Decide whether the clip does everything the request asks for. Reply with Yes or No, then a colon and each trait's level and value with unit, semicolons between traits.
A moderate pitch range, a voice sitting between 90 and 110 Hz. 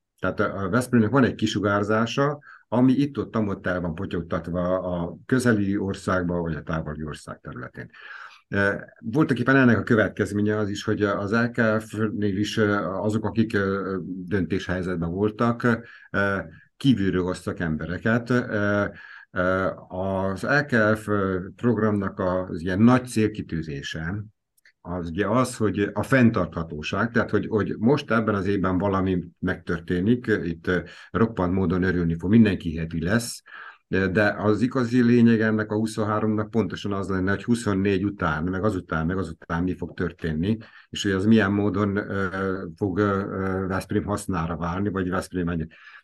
Yes: average, 3.3 semitones; low, 100 Hz